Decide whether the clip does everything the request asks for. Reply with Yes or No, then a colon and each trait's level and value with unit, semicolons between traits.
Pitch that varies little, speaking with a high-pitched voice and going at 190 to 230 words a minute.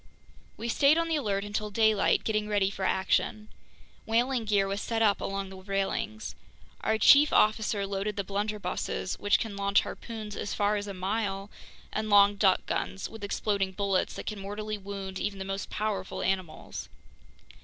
No: narrow, 1.7 semitones; high, 205 Hz; average, 170 wpm